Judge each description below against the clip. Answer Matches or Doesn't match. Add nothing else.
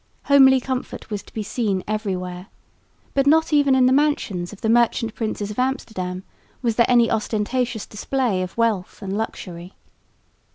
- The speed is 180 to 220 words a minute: Doesn't match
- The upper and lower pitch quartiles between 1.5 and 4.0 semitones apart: Doesn't match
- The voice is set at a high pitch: Matches